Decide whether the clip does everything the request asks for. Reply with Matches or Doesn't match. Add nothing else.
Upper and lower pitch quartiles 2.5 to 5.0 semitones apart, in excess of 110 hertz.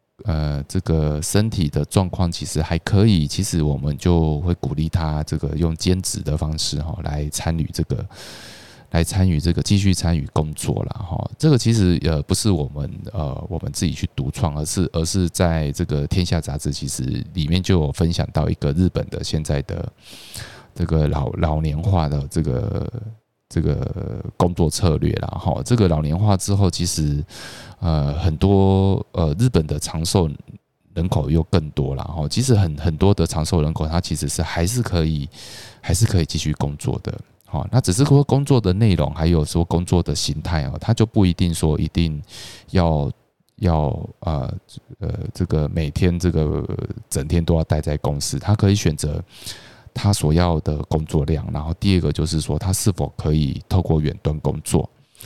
Doesn't match